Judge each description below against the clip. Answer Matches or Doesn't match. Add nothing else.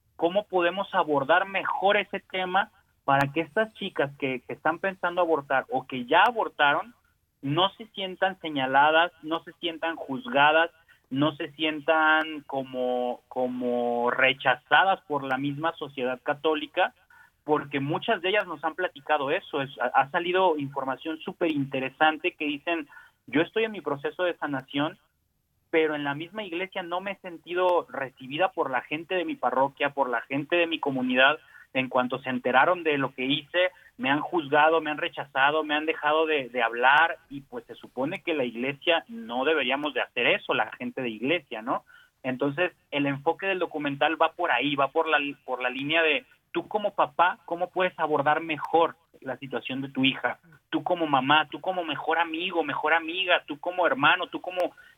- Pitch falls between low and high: Matches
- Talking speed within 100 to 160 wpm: Doesn't match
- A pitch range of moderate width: Matches